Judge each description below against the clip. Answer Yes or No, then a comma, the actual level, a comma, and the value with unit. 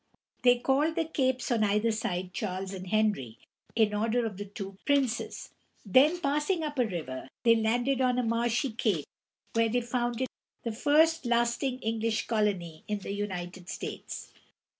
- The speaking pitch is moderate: No, high, 230 Hz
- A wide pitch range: No, average, 3.9 semitones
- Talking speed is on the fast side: No, average, 160 wpm